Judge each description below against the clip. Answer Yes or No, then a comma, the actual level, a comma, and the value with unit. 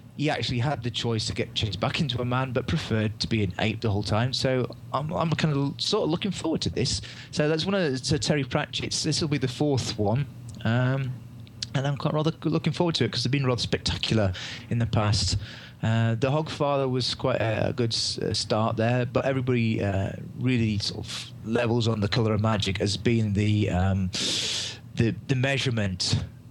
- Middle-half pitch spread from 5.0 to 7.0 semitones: No, average, 3.6 semitones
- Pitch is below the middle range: Yes, low, 120 Hz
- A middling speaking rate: No, fast, 210 wpm